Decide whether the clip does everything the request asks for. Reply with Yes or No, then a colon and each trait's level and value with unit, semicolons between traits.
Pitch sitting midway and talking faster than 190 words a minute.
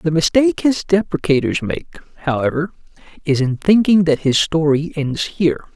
No: medium, 165 Hz; average, 145 wpm